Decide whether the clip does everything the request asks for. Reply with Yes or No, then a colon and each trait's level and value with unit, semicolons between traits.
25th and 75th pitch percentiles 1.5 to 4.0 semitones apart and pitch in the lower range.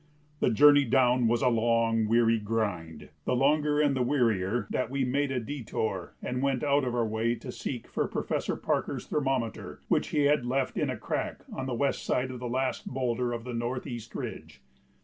Yes: average, 2.8 semitones; low, 125 Hz